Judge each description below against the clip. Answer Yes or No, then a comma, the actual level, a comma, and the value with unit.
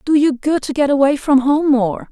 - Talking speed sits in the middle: No, fast, 255 wpm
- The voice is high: Yes, very high, 280 Hz